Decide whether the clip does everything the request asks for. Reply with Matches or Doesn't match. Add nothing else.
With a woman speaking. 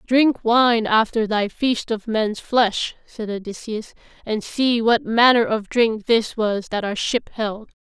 Matches